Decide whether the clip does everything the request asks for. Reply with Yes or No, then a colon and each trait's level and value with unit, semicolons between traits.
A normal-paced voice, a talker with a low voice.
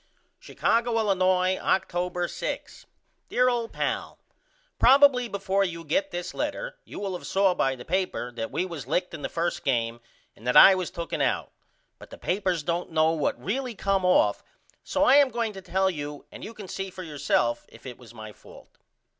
No: average, 190 wpm; medium, 185 Hz